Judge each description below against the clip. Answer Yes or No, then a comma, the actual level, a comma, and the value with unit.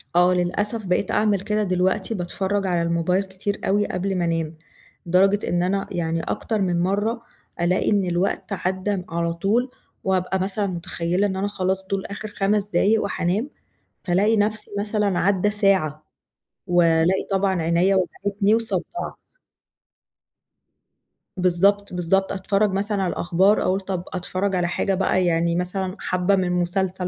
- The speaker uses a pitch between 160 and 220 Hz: Yes, high, 190 Hz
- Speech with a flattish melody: Yes, narrow, 2.2 semitones